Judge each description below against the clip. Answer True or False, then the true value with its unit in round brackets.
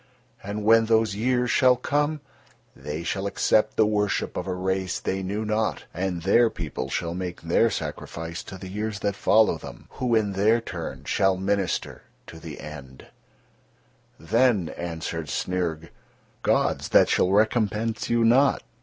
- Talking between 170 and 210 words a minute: False (155 wpm)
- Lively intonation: False (4.0 semitones)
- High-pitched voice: False (100 Hz)